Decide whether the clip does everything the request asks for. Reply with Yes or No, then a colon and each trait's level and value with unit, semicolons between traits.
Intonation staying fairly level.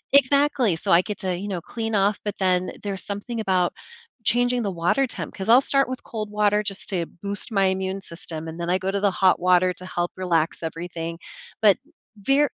No: average, 3.4 semitones